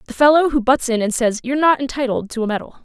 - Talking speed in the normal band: No, fast, 275 wpm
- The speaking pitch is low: No, very high, 255 Hz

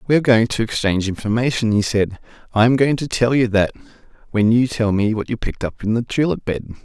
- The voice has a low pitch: Yes, low, 115 Hz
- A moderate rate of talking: No, fast, 235 wpm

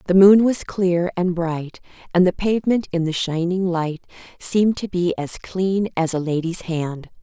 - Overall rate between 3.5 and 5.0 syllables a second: Yes, 4.6 syllables/s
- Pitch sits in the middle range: Yes, medium, 180 Hz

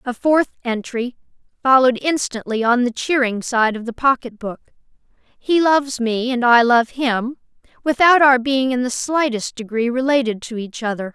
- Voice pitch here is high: Yes, very high, 250 Hz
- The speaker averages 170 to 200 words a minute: No, average, 160 wpm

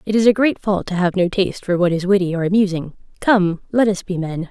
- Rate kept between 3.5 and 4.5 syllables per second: No, 6.0 syllables/s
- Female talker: Yes, female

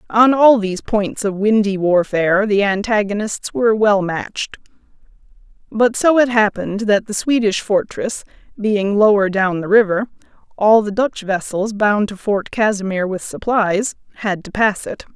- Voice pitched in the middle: No, high, 205 Hz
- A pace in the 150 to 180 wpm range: Yes, average, 155 wpm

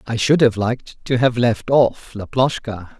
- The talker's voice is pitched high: No, low, 120 Hz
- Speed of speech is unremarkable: Yes, average, 180 wpm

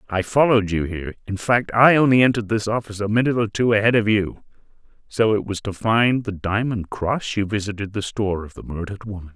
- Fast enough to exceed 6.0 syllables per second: Yes, 6.2 syllables/s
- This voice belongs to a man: Yes, male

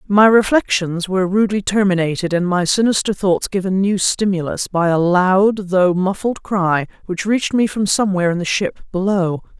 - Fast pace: No, average, 170 wpm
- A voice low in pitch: No, high, 190 Hz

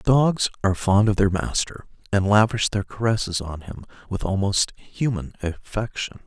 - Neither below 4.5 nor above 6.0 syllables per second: Yes, 5.0 syllables/s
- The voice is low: Yes, low, 100 Hz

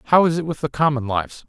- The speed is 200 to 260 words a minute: No, fast, 285 wpm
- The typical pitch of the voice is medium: Yes, medium, 145 Hz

